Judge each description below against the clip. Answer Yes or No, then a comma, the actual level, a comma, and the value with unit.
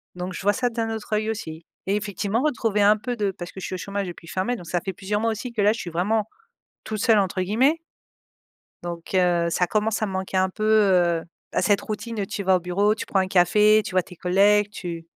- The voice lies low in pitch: No, high, 200 Hz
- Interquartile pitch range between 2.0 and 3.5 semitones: Yes, average, 2.9 semitones